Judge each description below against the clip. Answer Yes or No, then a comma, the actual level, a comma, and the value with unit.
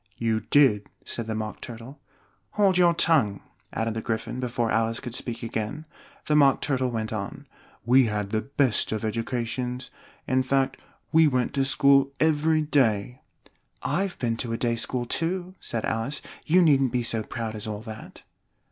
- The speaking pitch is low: Yes, low, 125 Hz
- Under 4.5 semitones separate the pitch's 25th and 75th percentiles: Yes, average, 3.9 semitones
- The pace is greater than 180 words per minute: No, average, 175 wpm